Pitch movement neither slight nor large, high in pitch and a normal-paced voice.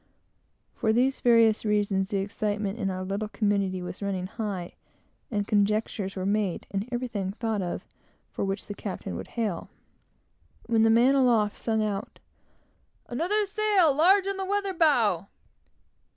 Yes: average, 3.8 semitones; high, 215 Hz; average, 150 wpm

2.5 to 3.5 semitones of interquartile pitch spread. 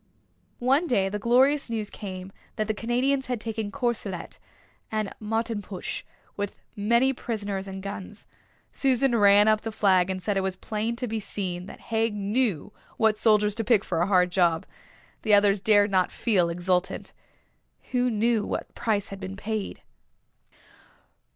Yes: average, 2.9 semitones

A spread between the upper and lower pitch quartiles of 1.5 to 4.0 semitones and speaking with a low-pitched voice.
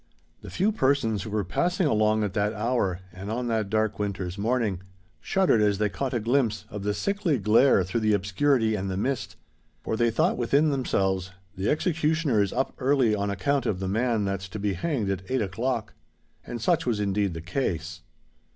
No: average, 4.6 semitones; low, 110 Hz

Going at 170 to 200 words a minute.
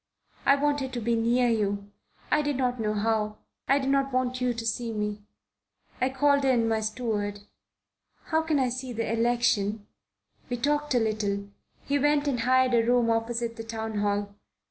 Yes: average, 180 wpm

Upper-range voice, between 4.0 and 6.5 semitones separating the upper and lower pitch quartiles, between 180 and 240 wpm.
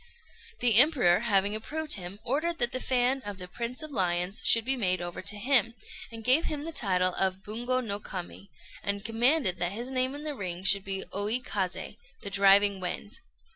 Yes: high, 210 Hz; average, 4.9 semitones; average, 195 wpm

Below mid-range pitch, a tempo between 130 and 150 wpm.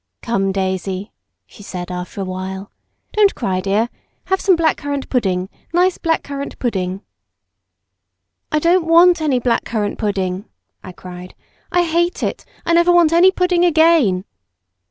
No: high, 240 Hz; average, 145 wpm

